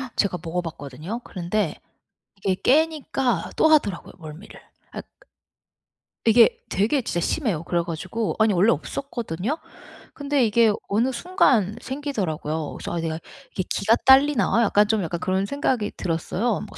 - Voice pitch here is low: No, high, 210 Hz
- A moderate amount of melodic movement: No, wide, 6.4 semitones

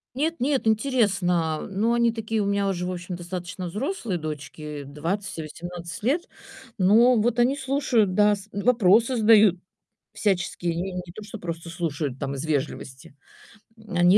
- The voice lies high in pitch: Yes, high, 195 Hz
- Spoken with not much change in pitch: No, average, 4.7 semitones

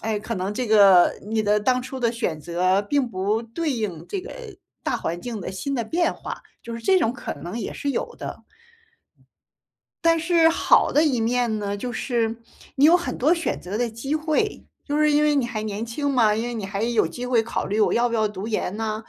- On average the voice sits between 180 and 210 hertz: No, high, 230 Hz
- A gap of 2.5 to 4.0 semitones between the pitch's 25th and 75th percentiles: No, average, 4.8 semitones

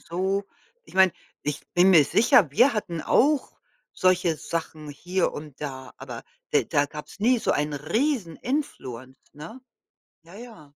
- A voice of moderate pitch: Yes, medium, 170 Hz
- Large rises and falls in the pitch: Yes, wide, 6.1 semitones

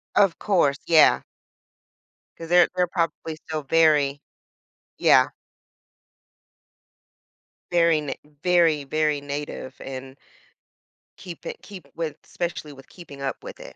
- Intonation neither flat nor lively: Yes, average, 3.2 semitones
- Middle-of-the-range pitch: Yes, medium, 155 Hz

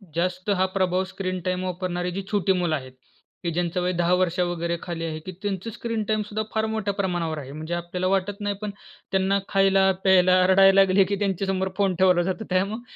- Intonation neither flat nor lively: No, narrow, 1.8 semitones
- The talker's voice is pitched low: No, medium, 185 Hz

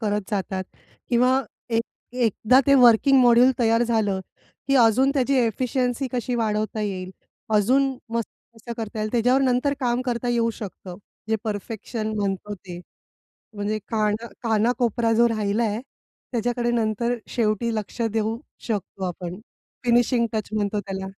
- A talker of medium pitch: No, high, 225 Hz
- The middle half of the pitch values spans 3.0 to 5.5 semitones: No, narrow, 2.6 semitones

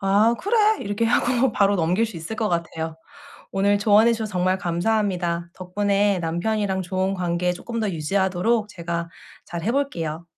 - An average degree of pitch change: Yes, average, 4.1 semitones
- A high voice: Yes, high, 195 Hz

